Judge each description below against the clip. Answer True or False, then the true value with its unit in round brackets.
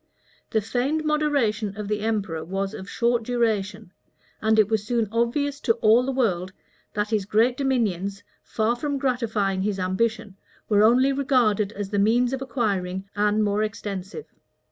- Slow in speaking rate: False (160 wpm)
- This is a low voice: False (220 Hz)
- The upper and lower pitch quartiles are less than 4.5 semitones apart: True (3.4 semitones)